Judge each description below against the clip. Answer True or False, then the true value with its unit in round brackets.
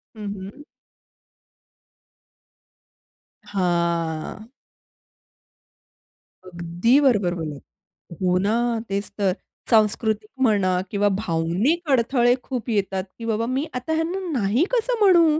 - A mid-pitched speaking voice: False (215 Hz)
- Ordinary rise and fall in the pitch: False (5.9 semitones)